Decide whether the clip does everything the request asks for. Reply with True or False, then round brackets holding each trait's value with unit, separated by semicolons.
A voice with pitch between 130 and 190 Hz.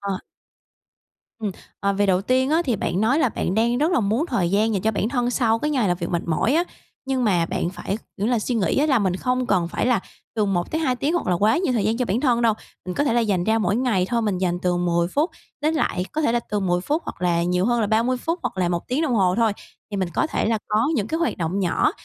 False (220 Hz)